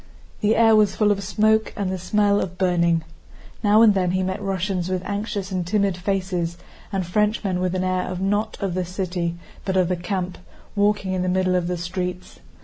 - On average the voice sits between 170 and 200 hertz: Yes, medium, 185 Hz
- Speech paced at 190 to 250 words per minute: Yes, average, 200 wpm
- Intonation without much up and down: Yes, narrow, 2.1 semitones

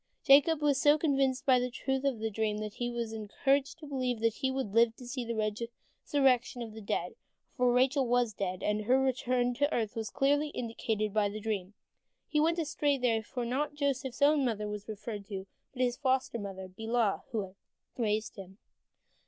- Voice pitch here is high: Yes, high, 240 Hz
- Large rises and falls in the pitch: No, average, 3.9 semitones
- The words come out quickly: No, average, 195 wpm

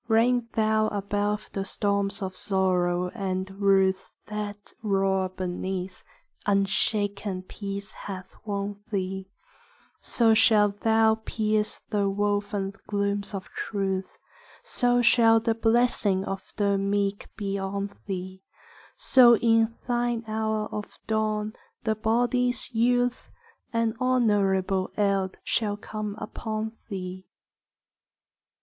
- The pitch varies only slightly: Yes, narrow, 2.3 semitones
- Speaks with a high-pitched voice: Yes, high, 205 Hz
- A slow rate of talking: Yes, slow, 110 wpm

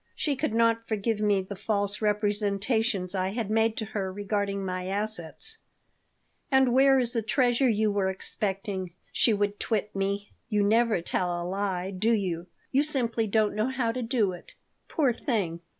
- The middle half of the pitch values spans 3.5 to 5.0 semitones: No, average, 2.9 semitones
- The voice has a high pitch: Yes, high, 210 Hz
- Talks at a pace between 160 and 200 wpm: Yes, average, 170 wpm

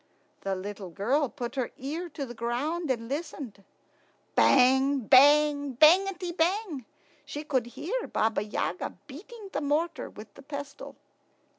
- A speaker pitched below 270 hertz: No, very high, 280 Hz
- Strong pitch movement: No, average, 4.8 semitones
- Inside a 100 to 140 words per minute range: Yes, slow, 135 wpm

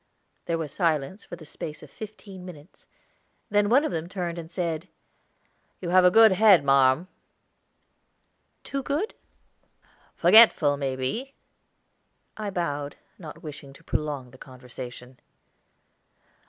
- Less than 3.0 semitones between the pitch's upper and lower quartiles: No, wide, 5.5 semitones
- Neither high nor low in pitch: Yes, medium, 165 Hz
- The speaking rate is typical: No, slow, 125 wpm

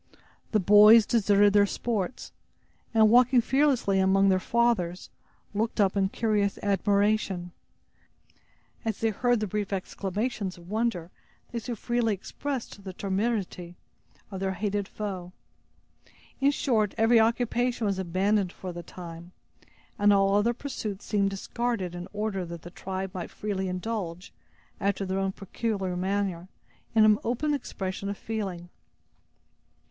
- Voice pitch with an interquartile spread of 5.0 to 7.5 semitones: No, average, 3.0 semitones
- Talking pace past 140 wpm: No, slow, 135 wpm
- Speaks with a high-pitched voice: Yes, high, 200 Hz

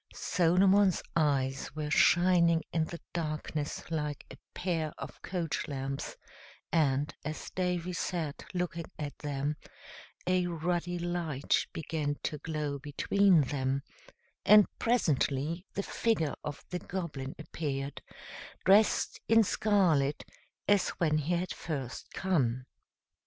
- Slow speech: Yes, slow, 115 wpm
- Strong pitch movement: No, average, 3.6 semitones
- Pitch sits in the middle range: Yes, medium, 160 Hz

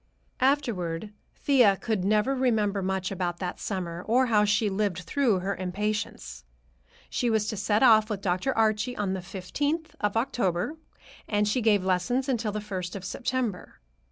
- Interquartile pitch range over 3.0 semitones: Yes, average, 3.9 semitones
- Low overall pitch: No, high, 210 Hz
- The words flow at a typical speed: Yes, average, 160 wpm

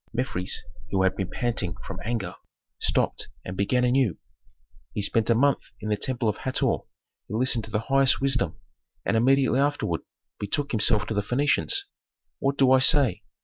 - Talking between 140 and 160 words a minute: No, average, 170 wpm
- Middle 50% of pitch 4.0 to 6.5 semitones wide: Yes, average, 4.3 semitones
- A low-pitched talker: Yes, low, 120 Hz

